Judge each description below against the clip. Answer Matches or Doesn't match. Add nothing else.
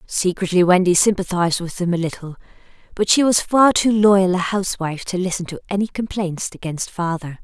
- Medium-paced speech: Matches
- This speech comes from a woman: Matches